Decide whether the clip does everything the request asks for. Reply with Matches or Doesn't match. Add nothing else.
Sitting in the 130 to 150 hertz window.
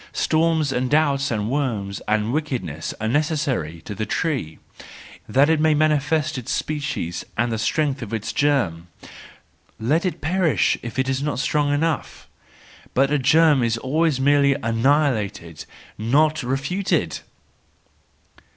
Matches